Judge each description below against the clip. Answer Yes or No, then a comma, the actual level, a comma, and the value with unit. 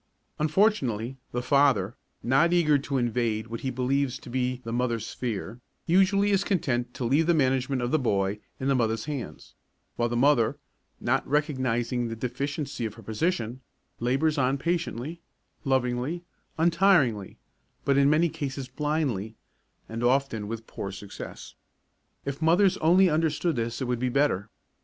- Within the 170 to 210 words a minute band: No, average, 150 wpm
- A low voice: Yes, low, 130 Hz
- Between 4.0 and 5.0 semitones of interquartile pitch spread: Yes, average, 4.5 semitones